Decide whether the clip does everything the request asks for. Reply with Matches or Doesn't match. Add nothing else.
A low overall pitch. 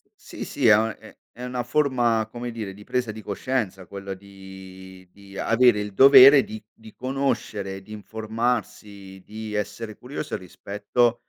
Matches